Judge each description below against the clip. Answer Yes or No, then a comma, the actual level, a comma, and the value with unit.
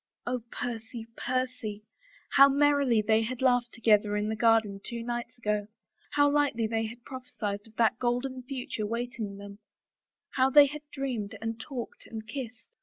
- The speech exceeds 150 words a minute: Yes, average, 165 wpm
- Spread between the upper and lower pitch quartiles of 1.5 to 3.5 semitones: Yes, average, 2.8 semitones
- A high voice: Yes, high, 235 Hz